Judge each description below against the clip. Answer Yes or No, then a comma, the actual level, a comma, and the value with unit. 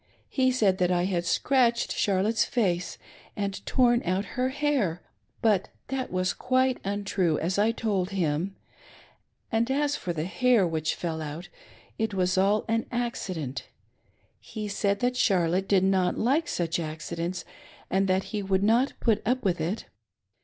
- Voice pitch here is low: No, high, 195 Hz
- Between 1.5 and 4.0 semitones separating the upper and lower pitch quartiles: No, average, 4.7 semitones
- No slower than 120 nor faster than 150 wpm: No, average, 160 wpm